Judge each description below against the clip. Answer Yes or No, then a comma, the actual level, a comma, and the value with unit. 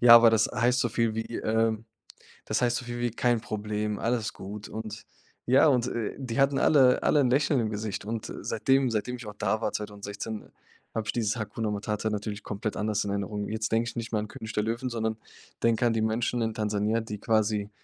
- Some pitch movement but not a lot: No, narrow, 2.1 semitones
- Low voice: Yes, low, 110 Hz